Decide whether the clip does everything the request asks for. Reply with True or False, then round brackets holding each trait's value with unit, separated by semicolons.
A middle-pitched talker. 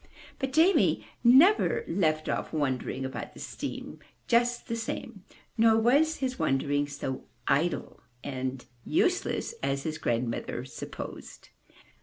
True (175 Hz)